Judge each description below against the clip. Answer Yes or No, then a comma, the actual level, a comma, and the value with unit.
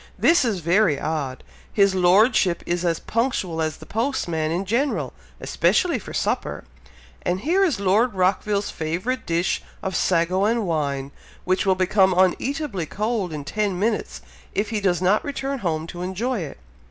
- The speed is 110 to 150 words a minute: No, average, 160 wpm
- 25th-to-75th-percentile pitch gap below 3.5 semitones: No, average, 4.5 semitones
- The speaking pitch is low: No, high, 190 Hz